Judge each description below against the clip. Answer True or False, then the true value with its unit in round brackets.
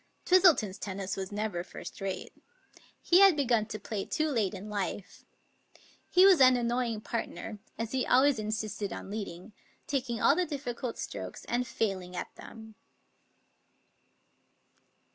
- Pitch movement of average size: True (4.4 semitones)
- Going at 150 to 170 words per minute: False (140 wpm)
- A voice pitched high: True (225 Hz)